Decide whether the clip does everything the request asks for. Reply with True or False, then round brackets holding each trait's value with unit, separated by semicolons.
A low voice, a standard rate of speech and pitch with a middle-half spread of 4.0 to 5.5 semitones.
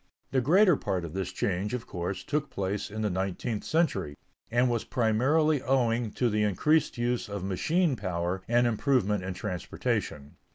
True (110 Hz; 165 wpm; 5.2 semitones)